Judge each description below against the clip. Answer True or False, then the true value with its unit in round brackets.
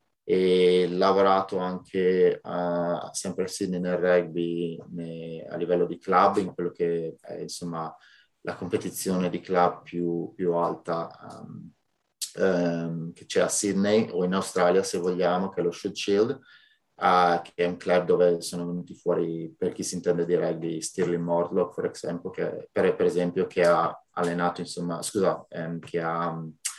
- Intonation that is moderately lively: False (1.3 semitones)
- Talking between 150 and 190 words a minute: True (165 wpm)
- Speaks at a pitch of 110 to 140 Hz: False (90 Hz)